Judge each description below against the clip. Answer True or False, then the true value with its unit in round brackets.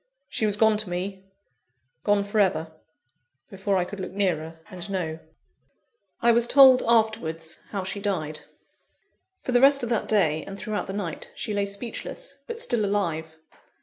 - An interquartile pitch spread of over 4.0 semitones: False (3.6 semitones)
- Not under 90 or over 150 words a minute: False (165 wpm)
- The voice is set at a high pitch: True (200 Hz)